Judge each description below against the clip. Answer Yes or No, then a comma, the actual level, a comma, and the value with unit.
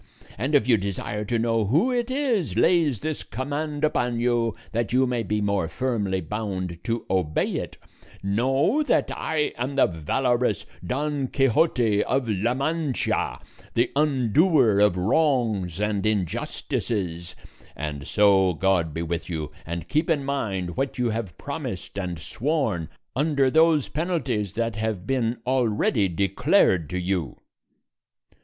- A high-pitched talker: No, low, 115 Hz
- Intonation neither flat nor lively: No, wide, 6.2 semitones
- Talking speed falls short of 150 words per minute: Yes, average, 140 wpm